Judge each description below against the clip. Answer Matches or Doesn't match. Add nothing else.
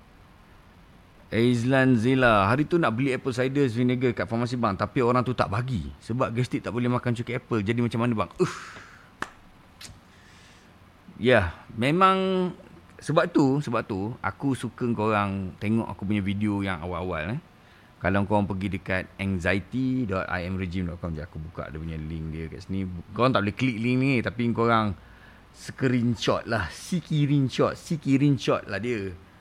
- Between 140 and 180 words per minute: Matches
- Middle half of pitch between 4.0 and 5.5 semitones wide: Matches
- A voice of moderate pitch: Doesn't match